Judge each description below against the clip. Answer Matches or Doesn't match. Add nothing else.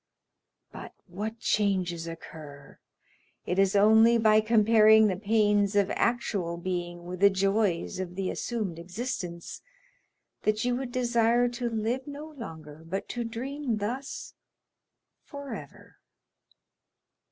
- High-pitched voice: Matches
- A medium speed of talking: Doesn't match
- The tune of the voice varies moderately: Matches